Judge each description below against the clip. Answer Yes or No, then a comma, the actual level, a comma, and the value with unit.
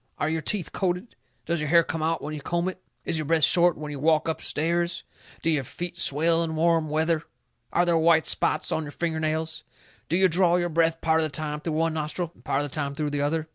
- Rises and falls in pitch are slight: Yes, narrow, 1.7 semitones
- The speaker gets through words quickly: Yes, fast, 250 wpm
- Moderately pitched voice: Yes, medium, 160 Hz